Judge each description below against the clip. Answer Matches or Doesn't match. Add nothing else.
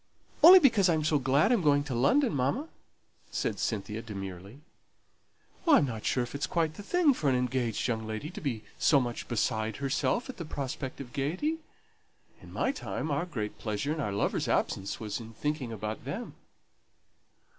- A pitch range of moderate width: Doesn't match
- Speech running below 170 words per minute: Doesn't match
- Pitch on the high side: Doesn't match